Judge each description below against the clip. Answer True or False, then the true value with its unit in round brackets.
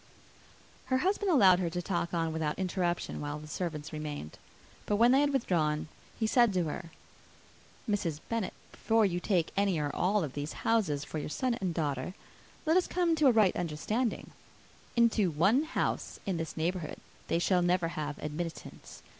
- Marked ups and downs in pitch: True (6.2 semitones)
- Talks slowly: False (175 wpm)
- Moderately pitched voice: True (180 Hz)